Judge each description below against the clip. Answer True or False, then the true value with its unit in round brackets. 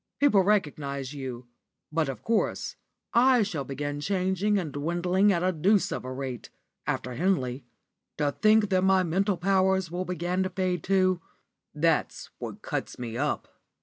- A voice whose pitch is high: False (180 Hz)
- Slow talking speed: False (155 wpm)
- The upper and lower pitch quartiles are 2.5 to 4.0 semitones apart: False (4.9 semitones)